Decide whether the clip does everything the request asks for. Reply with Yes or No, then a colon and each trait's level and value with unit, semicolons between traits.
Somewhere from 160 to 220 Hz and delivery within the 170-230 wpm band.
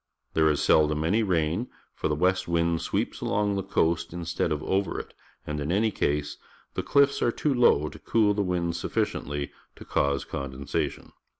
No: very low, 85 Hz; average, 180 wpm